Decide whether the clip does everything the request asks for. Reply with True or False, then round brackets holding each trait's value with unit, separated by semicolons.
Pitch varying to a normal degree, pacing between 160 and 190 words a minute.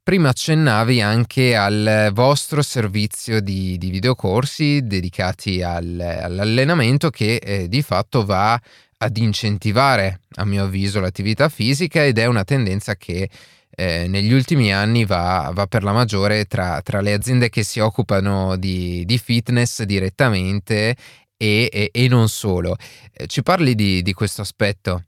False (4.2 semitones; 145 wpm)